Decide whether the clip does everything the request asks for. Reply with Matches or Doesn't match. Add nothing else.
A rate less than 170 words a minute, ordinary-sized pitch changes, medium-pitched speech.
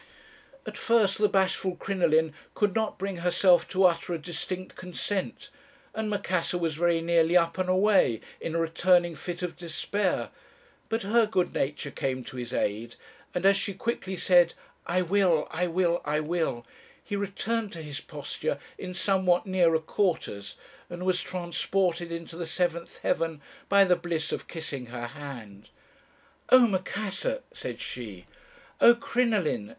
Matches